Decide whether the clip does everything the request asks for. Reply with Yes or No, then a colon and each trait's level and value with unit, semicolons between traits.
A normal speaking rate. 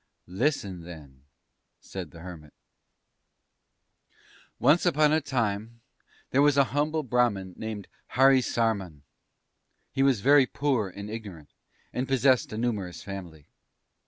No: slow, 115 wpm